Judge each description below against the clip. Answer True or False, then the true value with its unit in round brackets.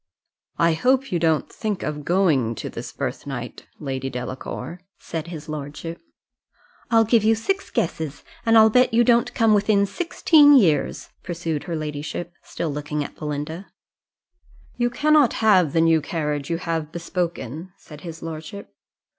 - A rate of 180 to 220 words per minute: False (155 wpm)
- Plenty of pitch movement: True (6.3 semitones)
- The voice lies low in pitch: False (170 Hz)